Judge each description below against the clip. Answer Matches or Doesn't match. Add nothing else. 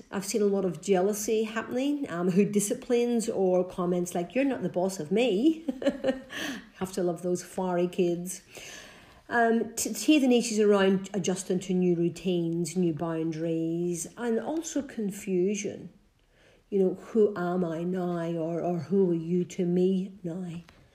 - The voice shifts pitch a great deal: Doesn't match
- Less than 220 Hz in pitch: Matches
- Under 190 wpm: Matches